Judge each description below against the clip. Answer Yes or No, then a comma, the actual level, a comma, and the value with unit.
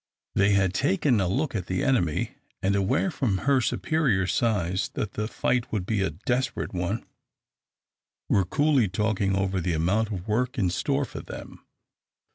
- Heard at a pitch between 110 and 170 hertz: No, low, 100 Hz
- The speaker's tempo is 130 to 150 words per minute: No, average, 165 wpm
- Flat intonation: No, average, 4.7 semitones